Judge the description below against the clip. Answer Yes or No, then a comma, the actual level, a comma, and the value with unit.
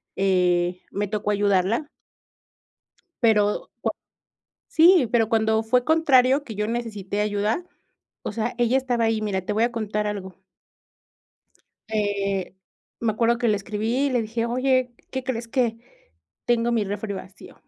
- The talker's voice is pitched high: Yes, high, 220 Hz